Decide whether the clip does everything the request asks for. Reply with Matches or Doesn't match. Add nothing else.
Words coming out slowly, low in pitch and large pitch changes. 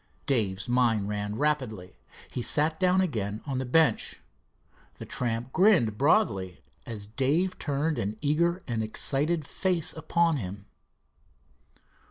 Matches